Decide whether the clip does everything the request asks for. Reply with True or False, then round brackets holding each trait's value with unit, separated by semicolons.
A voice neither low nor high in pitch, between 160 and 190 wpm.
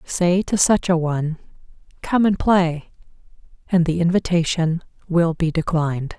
False (170 Hz; 135 wpm)